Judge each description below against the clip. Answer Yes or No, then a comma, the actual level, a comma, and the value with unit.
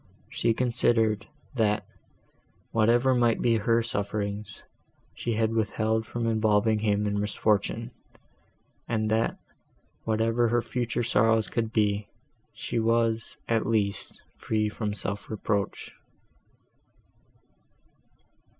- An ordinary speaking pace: No, slow, 105 wpm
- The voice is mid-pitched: No, low, 110 Hz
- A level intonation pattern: Yes, narrow, 1.6 semitones